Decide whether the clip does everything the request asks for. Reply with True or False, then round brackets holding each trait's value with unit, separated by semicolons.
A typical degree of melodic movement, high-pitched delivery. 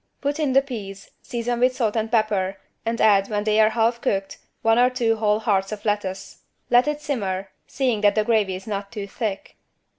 True (3.1 semitones; 215 Hz)